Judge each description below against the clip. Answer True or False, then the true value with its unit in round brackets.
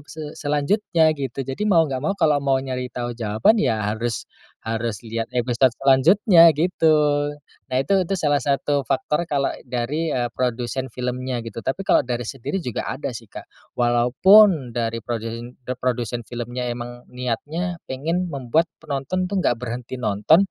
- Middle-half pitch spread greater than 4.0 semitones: True (4.5 semitones)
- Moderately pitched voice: False (130 Hz)